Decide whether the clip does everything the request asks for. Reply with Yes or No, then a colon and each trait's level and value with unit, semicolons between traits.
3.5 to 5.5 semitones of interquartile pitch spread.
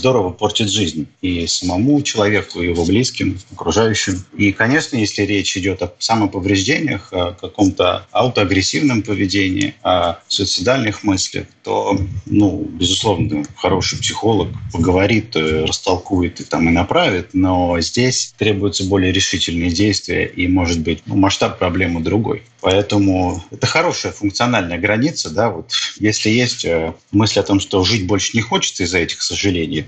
No: average, 2.9 semitones